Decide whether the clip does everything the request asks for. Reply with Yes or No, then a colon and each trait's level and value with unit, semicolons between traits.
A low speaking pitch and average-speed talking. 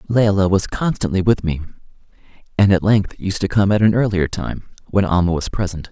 Yes: very low, 95 Hz; average, 195 wpm